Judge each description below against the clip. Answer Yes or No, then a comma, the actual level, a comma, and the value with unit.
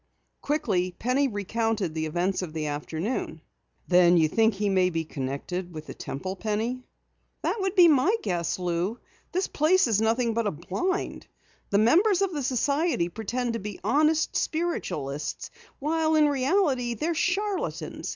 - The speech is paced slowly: No, average, 155 wpm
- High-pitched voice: Yes, high, 225 Hz